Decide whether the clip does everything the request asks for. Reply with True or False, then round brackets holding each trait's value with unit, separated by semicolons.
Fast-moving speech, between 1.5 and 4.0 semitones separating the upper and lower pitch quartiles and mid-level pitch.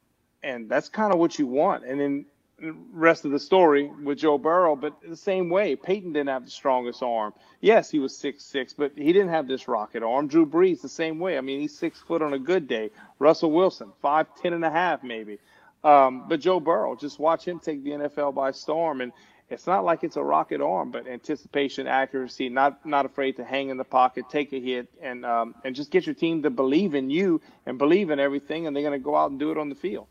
True (245 wpm; 3.5 semitones; 145 Hz)